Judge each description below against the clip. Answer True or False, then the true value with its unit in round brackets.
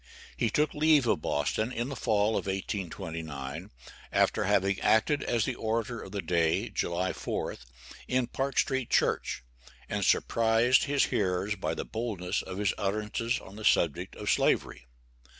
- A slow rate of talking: False (155 wpm)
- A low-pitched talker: True (105 Hz)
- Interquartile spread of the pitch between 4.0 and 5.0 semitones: True (4.4 semitones)